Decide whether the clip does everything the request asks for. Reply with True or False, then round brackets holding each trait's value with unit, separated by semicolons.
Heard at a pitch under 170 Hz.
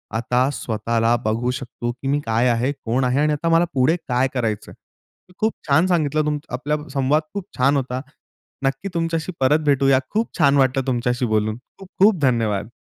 True (135 Hz)